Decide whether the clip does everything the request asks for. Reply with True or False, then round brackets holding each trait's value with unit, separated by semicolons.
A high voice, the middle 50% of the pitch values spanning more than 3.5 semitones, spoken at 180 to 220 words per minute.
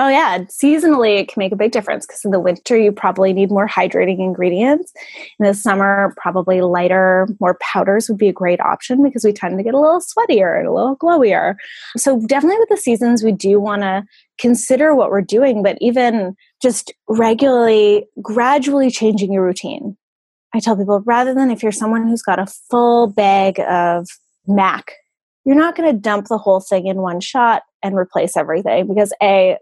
True (215 Hz; 4.5 semitones; 190 wpm)